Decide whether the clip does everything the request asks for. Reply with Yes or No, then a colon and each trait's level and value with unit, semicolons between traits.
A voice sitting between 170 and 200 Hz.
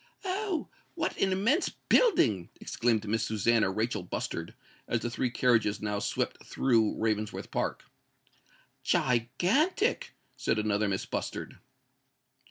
No: low, 115 Hz